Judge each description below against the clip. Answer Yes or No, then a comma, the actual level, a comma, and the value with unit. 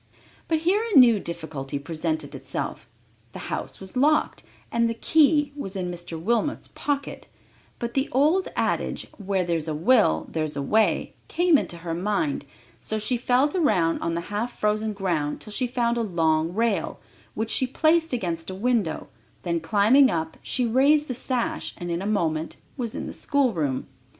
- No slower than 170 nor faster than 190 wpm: Yes, average, 175 wpm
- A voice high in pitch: Yes, high, 210 Hz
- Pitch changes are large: Yes, wide, 7.3 semitones